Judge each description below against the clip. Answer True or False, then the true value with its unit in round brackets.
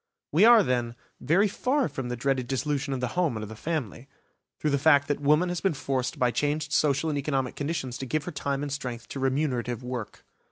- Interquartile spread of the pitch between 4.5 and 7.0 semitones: False (3.4 semitones)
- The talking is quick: True (220 wpm)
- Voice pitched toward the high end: False (140 Hz)